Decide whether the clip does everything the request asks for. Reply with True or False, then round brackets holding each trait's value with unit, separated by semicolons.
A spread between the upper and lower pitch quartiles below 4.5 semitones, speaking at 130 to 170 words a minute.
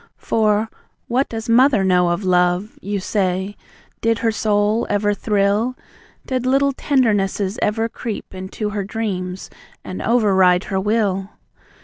True (3.0 semitones; 135 wpm)